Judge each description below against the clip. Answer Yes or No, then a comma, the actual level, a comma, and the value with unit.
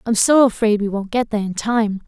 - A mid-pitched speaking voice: No, high, 215 Hz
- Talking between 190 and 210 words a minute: No, fast, 260 wpm